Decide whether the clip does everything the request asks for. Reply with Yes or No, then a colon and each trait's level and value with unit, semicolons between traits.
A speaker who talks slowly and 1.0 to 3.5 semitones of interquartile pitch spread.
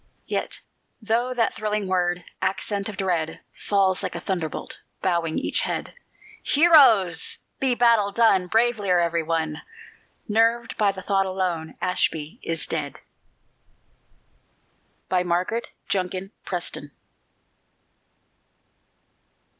No: slow, 100 wpm; average, 4.1 semitones